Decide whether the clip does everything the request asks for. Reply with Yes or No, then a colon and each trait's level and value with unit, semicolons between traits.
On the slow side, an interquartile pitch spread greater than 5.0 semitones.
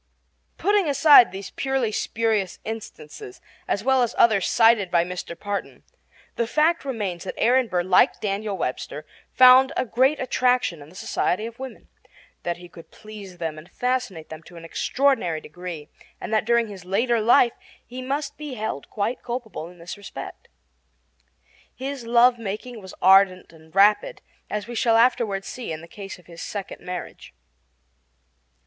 No: average, 165 wpm; wide, 5.6 semitones